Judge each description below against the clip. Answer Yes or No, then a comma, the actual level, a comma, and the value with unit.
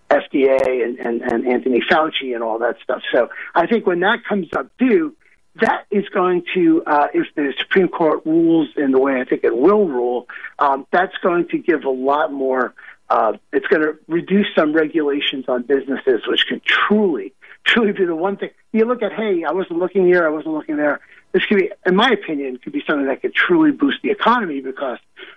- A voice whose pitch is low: No, medium, 185 Hz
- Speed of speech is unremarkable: No, fast, 210 wpm